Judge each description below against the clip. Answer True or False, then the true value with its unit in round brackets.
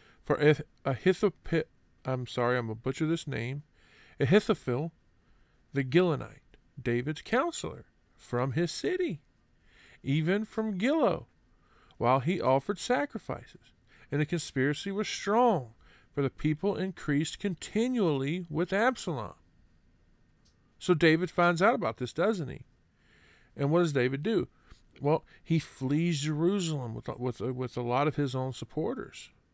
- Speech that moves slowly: True (130 wpm)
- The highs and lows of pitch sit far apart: True (6.0 semitones)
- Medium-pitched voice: True (150 Hz)